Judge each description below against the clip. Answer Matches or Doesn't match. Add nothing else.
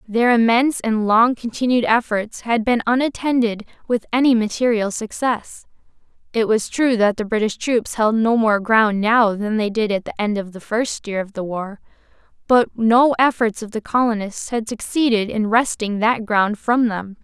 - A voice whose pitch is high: Matches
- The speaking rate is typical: Matches